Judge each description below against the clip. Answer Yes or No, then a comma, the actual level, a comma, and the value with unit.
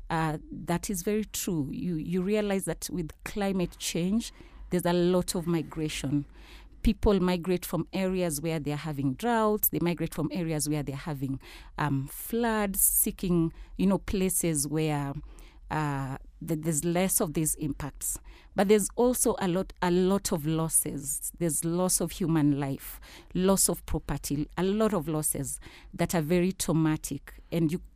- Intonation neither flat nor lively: Yes, average, 3.6 semitones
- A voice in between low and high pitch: Yes, medium, 170 Hz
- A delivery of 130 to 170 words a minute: Yes, average, 160 wpm